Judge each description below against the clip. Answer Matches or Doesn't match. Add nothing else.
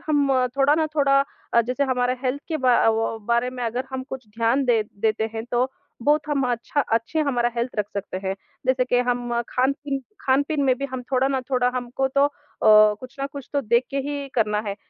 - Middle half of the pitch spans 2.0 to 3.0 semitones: Matches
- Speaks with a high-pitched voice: Matches